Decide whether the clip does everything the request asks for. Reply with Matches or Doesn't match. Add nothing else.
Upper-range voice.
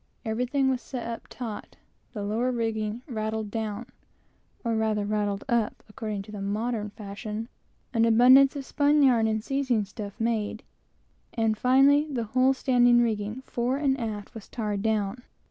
Matches